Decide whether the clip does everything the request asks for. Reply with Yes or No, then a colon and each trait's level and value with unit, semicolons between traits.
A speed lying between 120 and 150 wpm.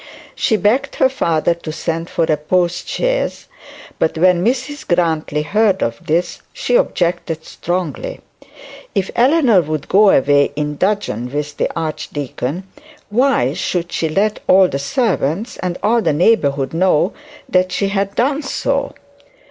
Yes: average, 140 wpm